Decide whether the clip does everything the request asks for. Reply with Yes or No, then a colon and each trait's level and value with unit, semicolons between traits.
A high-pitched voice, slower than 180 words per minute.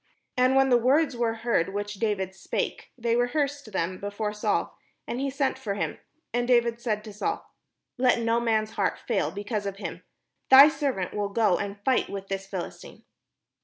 No: high, 225 Hz; average, 185 wpm